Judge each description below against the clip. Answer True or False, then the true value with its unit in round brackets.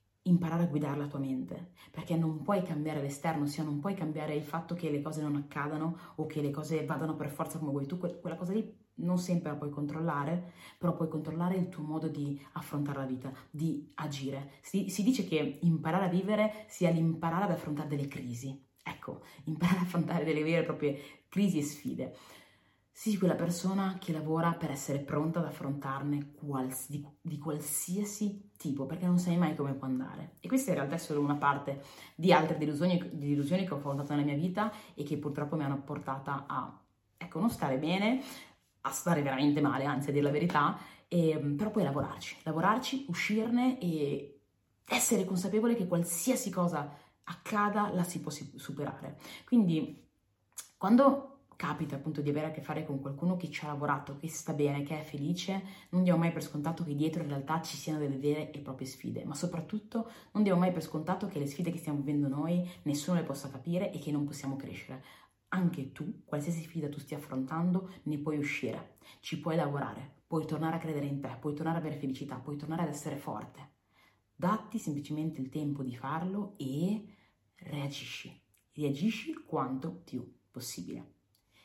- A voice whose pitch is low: False (155 Hz)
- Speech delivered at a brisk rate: True (190 wpm)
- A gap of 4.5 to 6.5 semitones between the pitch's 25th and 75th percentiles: False (3.4 semitones)